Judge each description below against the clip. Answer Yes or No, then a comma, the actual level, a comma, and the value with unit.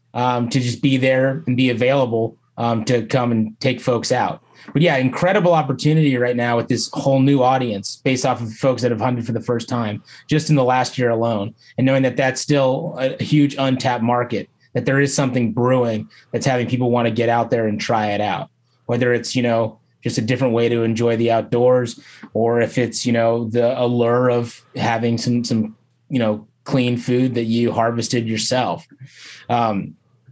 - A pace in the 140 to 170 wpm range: No, average, 200 wpm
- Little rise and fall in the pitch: Yes, narrow, 2.0 semitones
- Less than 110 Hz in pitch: No, low, 125 Hz